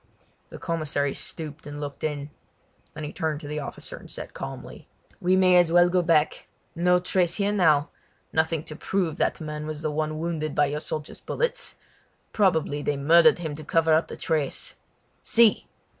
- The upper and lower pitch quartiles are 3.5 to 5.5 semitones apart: No, average, 2.8 semitones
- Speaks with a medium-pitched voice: Yes, medium, 160 Hz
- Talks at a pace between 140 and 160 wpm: No, average, 180 wpm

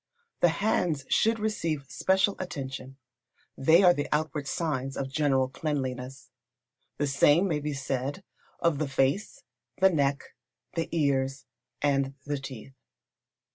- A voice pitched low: No, medium, 145 Hz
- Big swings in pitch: No, average, 3.7 semitones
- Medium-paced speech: No, slow, 130 wpm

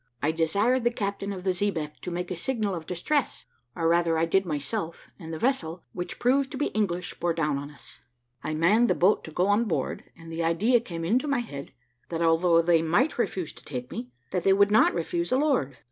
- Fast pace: Yes, fast, 225 wpm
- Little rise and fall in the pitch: No, average, 4.6 semitones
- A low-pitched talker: No, medium, 175 Hz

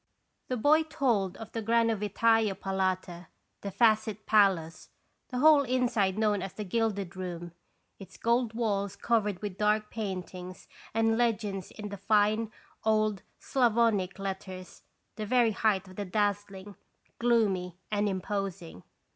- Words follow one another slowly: Yes, slow, 130 wpm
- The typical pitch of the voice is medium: No, high, 210 Hz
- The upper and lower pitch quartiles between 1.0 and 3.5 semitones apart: Yes, average, 2.8 semitones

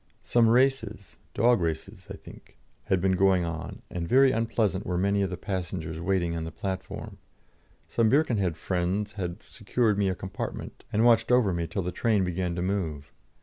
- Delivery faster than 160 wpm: Yes, average, 180 wpm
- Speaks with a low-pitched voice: Yes, very low, 95 Hz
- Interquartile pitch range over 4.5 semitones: No, average, 4.0 semitones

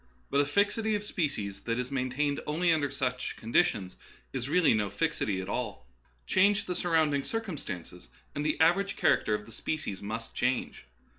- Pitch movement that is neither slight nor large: No, wide, 7.2 semitones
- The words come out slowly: No, average, 175 wpm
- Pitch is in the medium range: Yes, medium, 145 Hz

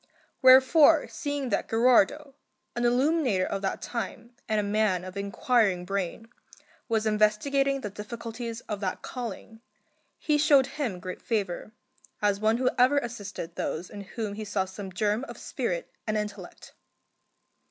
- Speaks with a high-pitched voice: Yes, high, 220 Hz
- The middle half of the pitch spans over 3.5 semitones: Yes, average, 4.2 semitones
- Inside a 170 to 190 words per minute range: No, average, 145 wpm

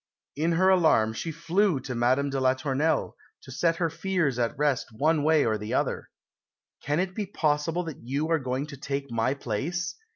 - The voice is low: No, medium, 145 Hz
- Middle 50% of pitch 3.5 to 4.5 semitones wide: Yes, average, 4.2 semitones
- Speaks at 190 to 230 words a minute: Yes, average, 195 wpm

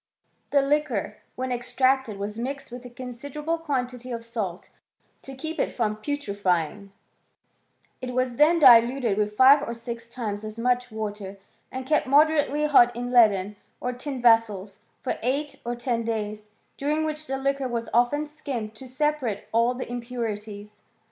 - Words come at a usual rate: Yes, average, 155 wpm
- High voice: Yes, high, 245 Hz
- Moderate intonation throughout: Yes, average, 4.0 semitones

